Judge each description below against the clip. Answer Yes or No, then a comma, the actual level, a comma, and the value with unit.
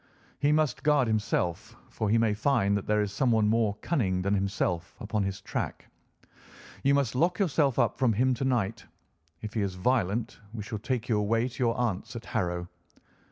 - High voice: No, low, 110 Hz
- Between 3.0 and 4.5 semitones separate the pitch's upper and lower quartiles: Yes, average, 3.9 semitones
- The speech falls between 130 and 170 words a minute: No, average, 190 wpm